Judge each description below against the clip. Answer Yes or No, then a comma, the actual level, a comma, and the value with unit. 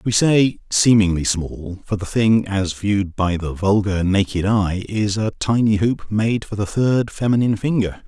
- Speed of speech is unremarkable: Yes, average, 180 wpm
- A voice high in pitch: No, low, 105 Hz